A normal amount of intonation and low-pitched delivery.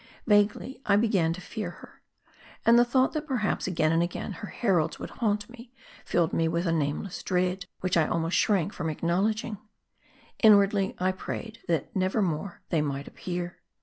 No: average, 4.0 semitones; medium, 185 Hz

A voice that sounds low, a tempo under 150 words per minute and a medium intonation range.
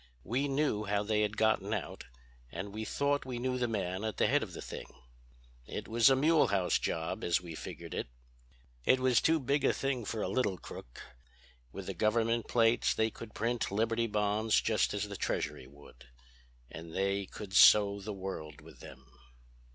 No: low, 110 Hz; average, 185 wpm; average, 3.4 semitones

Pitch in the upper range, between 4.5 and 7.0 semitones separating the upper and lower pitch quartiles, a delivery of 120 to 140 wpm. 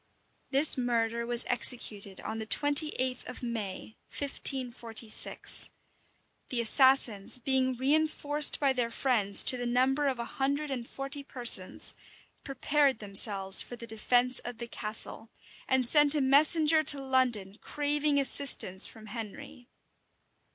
No: very high, 250 Hz; average, 3.5 semitones; slow, 135 wpm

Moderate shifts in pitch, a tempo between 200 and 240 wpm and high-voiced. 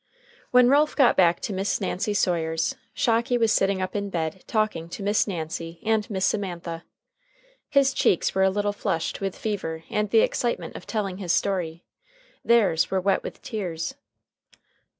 No: average, 4.0 semitones; average, 165 wpm; high, 195 Hz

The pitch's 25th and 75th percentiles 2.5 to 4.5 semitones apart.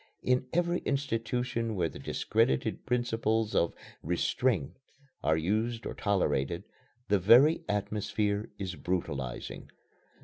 No: average, 5.2 semitones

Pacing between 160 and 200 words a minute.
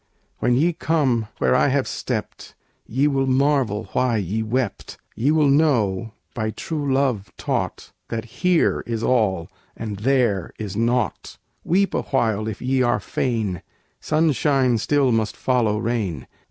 No: average, 140 wpm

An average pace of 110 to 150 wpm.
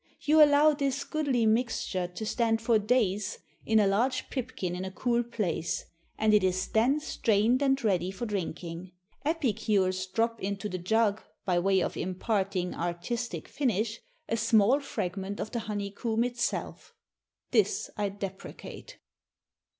Yes: average, 140 wpm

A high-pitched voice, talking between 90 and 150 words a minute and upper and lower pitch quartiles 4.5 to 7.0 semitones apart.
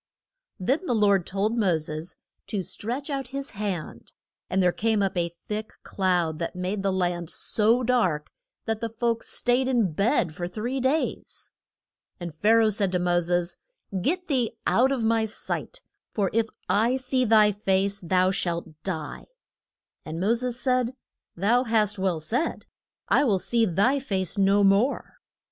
No: high, 210 Hz; average, 165 wpm; average, 4.8 semitones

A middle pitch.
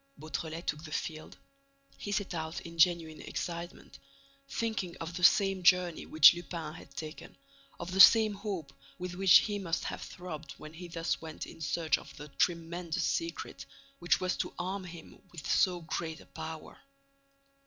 Yes: medium, 170 Hz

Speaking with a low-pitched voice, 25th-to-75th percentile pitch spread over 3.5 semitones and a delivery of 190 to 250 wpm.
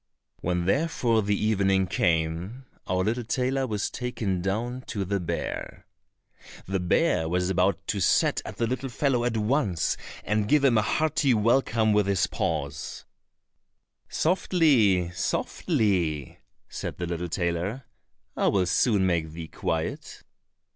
No: low, 100 Hz; wide, 5.4 semitones; slow, 135 wpm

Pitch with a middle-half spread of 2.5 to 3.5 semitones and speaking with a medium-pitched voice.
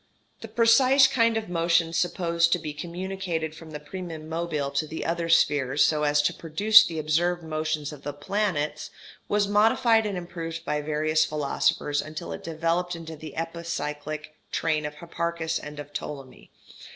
Yes: average, 2.8 semitones; medium, 165 Hz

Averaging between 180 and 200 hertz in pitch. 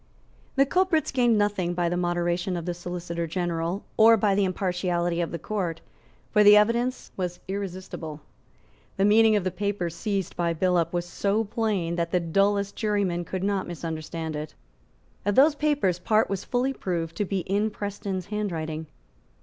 Yes: medium, 185 Hz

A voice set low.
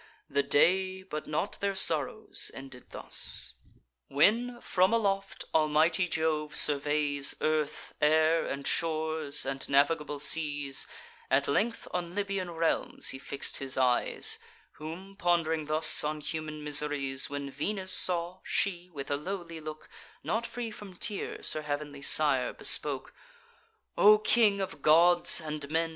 No: medium, 155 Hz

